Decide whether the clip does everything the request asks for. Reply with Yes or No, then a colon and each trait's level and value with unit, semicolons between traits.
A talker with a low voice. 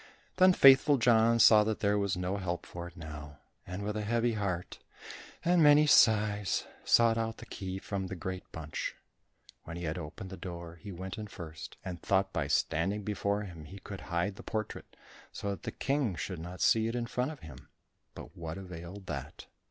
Yes: low, 100 Hz